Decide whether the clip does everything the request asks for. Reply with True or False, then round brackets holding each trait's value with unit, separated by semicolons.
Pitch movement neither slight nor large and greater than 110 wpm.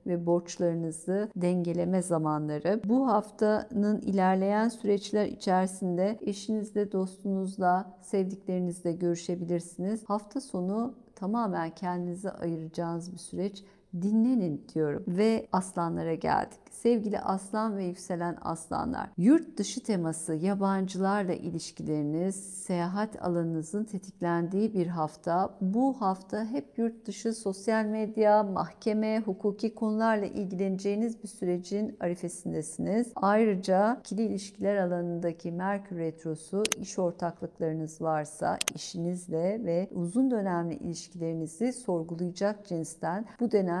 False (3.5 semitones; 100 wpm)